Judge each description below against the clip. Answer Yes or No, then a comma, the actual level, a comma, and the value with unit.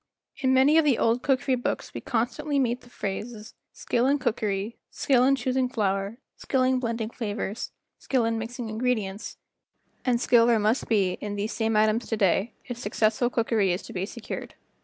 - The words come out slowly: No, average, 180 wpm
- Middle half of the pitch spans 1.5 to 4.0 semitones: Yes, average, 3.0 semitones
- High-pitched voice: Yes, high, 230 Hz